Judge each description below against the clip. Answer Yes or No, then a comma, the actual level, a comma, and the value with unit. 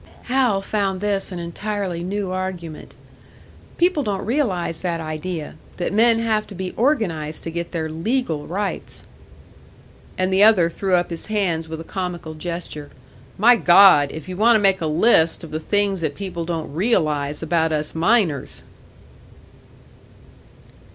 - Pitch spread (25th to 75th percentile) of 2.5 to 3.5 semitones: No, average, 4.1 semitones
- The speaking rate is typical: Yes, average, 150 wpm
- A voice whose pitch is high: No, medium, 180 Hz